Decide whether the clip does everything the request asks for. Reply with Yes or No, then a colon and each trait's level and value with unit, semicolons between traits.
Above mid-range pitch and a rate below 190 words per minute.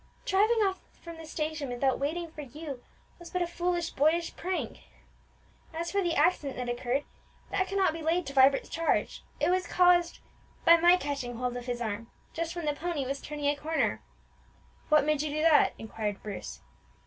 No: very high, 310 Hz; average, 195 wpm